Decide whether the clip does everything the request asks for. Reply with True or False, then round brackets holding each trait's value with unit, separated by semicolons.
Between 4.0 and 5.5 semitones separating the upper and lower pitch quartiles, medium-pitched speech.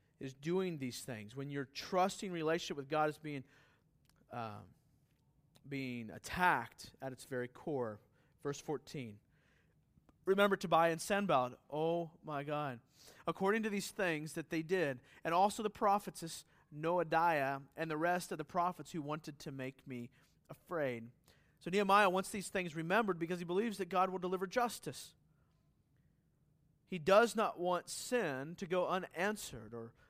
True (5.1 semitones; 160 Hz)